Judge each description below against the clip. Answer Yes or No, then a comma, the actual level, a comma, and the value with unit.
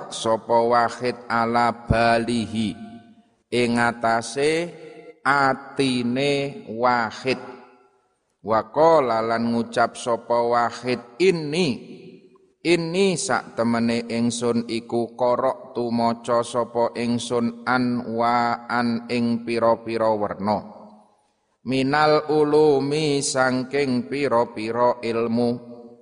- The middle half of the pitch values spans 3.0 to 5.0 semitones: No, narrow, 2.4 semitones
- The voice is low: Yes, low, 120 Hz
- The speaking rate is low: Yes, slow, 75 wpm